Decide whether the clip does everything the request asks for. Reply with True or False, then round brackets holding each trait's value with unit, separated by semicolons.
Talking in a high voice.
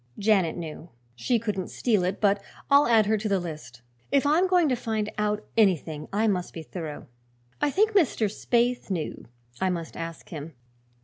True (205 Hz)